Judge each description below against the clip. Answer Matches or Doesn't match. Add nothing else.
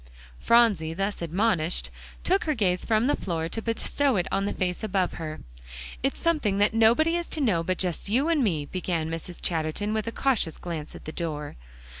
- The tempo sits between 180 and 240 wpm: Matches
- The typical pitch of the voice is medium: Doesn't match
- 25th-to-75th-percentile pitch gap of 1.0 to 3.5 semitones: Doesn't match